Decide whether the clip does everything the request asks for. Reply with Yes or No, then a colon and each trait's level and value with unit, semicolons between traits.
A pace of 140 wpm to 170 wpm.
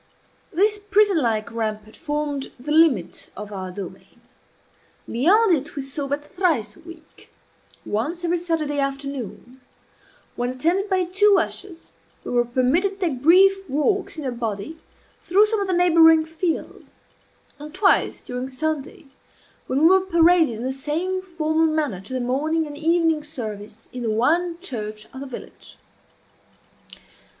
Yes: average, 150 wpm